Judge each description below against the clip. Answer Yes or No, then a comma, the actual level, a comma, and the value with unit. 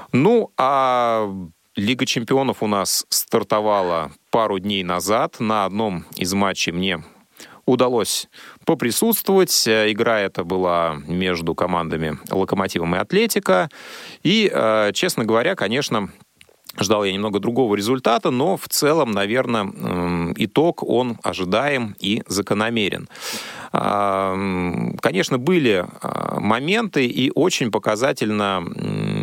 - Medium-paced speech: No, slow, 100 wpm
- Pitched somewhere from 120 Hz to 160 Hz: No, low, 105 Hz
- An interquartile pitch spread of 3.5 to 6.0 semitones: Yes, average, 5.2 semitones